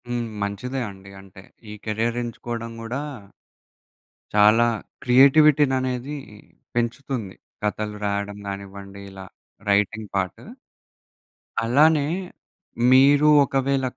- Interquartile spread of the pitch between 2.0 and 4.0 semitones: No, average, 4.6 semitones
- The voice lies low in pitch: Yes, low, 115 Hz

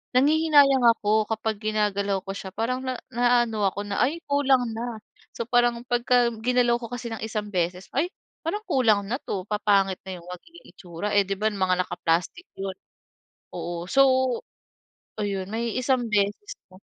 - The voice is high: Yes, high, 220 Hz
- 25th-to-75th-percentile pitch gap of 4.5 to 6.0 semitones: No, average, 4.0 semitones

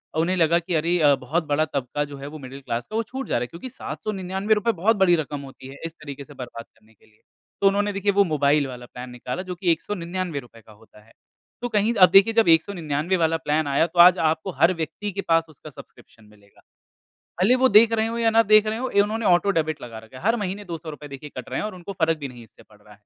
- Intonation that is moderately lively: No, wide, 6.1 semitones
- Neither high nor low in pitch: Yes, medium, 165 Hz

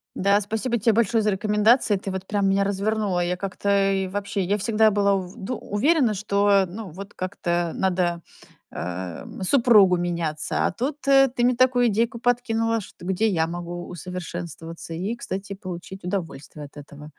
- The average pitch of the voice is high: Yes, high, 195 Hz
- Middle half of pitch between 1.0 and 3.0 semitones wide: No, average, 3.7 semitones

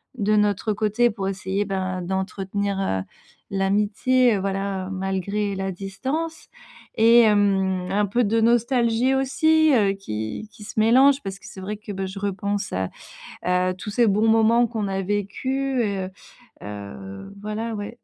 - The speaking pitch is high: Yes, high, 205 Hz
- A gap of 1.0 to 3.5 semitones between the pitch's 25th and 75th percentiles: Yes, average, 3.0 semitones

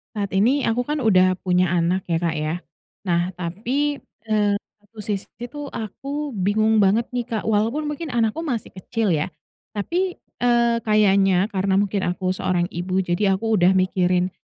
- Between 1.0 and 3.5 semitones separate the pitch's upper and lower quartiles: No, average, 4.3 semitones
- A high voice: Yes, high, 205 Hz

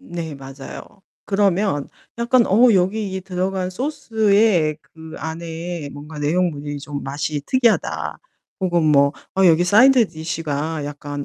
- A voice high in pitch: No, medium, 170 Hz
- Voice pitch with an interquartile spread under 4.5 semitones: No, average, 5.2 semitones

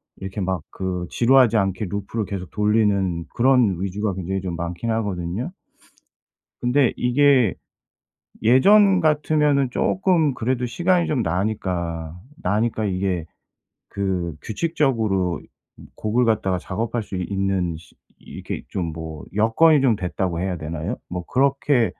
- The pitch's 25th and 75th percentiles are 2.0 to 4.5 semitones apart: No, wide, 5.6 semitones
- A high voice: No, low, 105 Hz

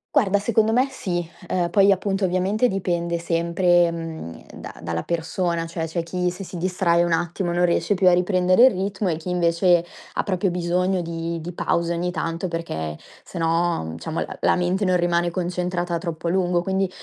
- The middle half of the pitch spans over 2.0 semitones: No, narrow, 1.7 semitones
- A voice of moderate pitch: Yes, medium, 175 Hz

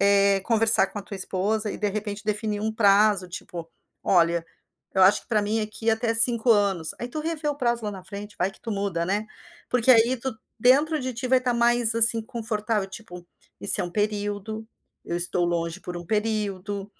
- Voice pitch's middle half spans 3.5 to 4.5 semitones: No, average, 2.8 semitones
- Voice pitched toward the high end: Yes, high, 210 Hz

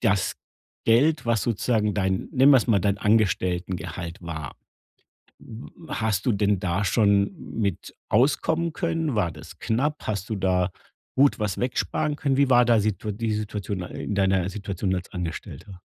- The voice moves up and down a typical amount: Yes, average, 4.2 semitones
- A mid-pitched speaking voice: No, low, 105 Hz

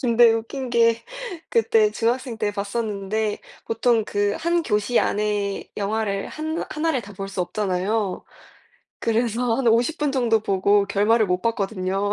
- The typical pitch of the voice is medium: No, high, 220 Hz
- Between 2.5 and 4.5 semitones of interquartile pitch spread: Yes, average, 3.0 semitones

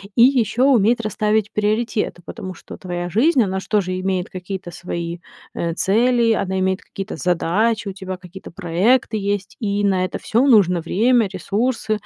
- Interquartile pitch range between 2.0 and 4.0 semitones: Yes, average, 3.4 semitones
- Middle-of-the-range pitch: No, high, 200 Hz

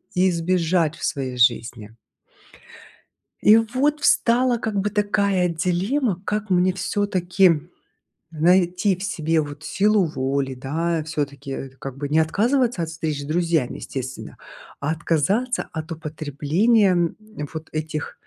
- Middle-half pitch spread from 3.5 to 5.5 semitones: Yes, average, 5.0 semitones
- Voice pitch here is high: No, medium, 170 Hz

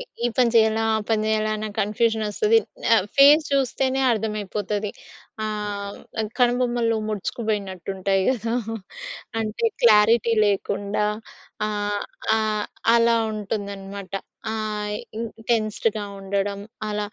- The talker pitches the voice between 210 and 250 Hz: Yes, high, 215 Hz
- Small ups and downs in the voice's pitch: Yes, narrow, 2.0 semitones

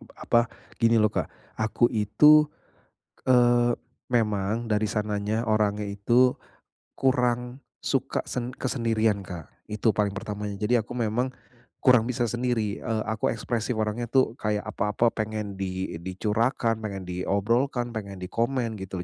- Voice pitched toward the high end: No, low, 110 Hz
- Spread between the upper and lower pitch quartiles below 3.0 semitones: Yes, narrow, 2.6 semitones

